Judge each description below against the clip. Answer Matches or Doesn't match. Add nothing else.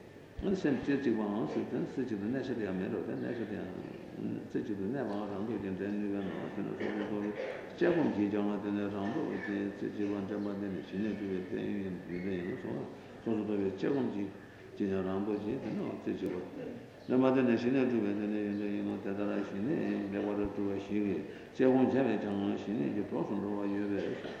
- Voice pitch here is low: Matches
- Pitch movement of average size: Doesn't match